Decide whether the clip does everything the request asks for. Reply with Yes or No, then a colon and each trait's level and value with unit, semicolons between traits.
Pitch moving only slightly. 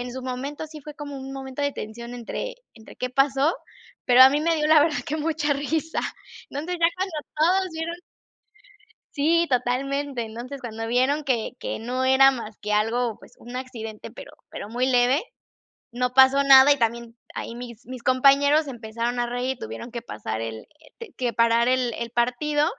No: average, 3.4 semitones